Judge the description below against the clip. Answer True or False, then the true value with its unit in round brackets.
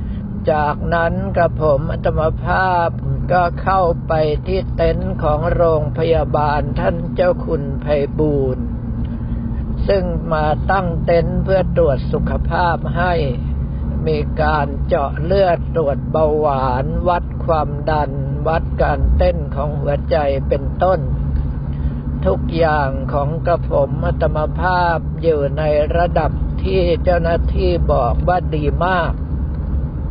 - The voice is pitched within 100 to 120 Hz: False (130 Hz)